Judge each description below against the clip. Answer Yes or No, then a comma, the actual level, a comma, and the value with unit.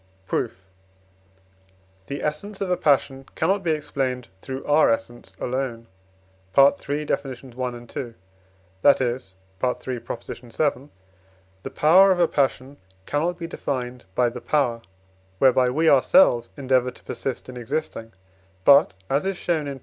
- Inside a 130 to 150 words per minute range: Yes, average, 140 wpm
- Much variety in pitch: No, average, 3.4 semitones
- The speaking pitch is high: No, low, 135 Hz